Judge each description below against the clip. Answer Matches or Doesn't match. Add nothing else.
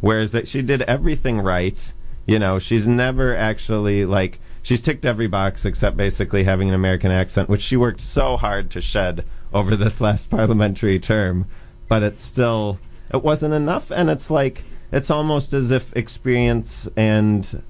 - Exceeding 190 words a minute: Doesn't match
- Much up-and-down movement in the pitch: Doesn't match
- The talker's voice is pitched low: Matches